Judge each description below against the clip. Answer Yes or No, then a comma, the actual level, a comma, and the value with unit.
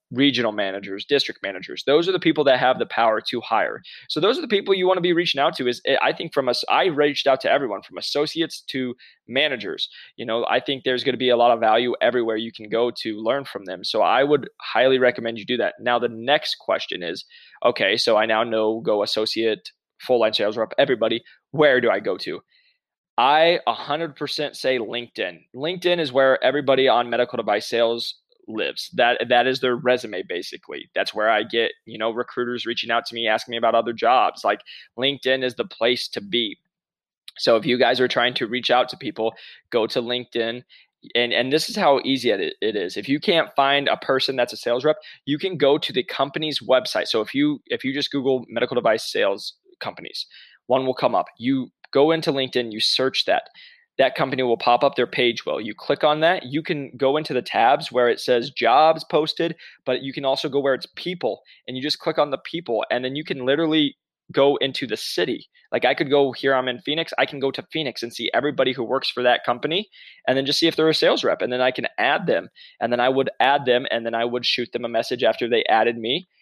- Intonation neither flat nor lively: Yes, average, 4.4 semitones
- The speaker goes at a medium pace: No, fast, 230 wpm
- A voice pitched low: Yes, low, 130 Hz